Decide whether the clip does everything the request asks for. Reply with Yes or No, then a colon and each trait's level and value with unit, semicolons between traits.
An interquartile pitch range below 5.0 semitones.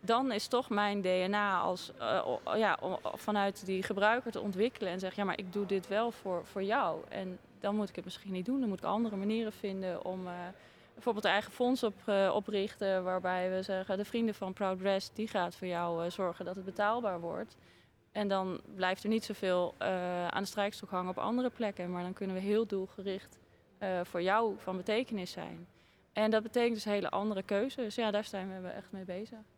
Yes: narrow, 2.5 semitones